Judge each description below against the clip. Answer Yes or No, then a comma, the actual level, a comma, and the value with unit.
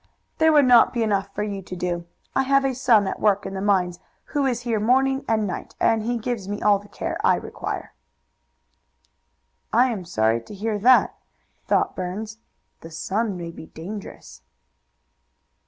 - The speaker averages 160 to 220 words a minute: Yes, average, 175 wpm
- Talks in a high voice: Yes, high, 210 Hz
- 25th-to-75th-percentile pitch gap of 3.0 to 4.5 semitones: Yes, average, 4.2 semitones